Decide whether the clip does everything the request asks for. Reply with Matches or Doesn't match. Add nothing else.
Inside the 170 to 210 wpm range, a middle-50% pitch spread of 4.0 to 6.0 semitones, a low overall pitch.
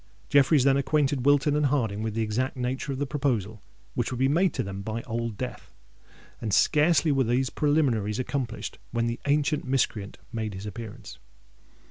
Matches